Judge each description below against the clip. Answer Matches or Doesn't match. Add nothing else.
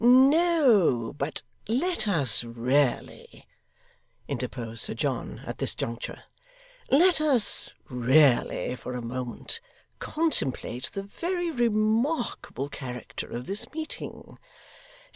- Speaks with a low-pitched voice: Doesn't match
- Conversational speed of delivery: Doesn't match